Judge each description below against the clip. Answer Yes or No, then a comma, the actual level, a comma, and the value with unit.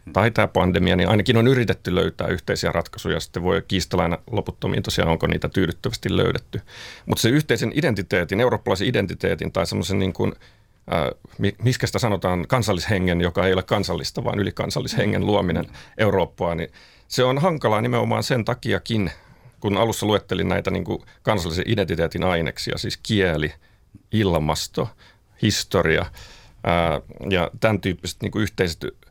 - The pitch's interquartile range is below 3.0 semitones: No, average, 4.1 semitones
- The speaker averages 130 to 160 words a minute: Yes, average, 140 wpm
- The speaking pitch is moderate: No, low, 100 Hz